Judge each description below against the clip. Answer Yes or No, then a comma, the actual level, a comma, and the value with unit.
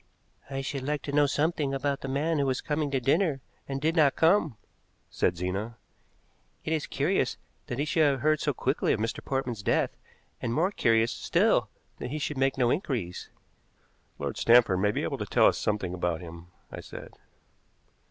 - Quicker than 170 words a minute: Yes, average, 190 wpm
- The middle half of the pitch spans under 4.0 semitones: No, average, 4.6 semitones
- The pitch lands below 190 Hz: Yes, low, 135 Hz